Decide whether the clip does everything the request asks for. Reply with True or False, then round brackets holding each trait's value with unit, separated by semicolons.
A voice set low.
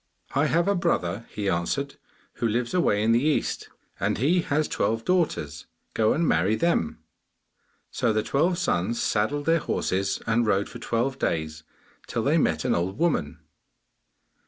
True (115 Hz)